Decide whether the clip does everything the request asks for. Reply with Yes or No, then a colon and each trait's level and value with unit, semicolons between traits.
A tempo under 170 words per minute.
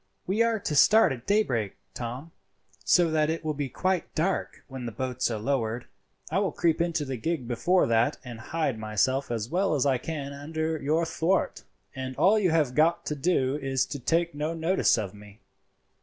No: average, 195 wpm